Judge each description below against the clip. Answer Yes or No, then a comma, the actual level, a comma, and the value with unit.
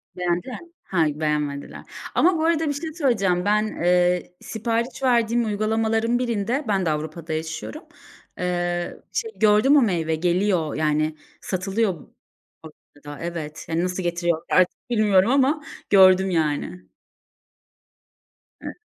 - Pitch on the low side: No, medium, 185 Hz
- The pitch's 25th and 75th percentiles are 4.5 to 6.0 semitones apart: Yes, wide, 5.5 semitones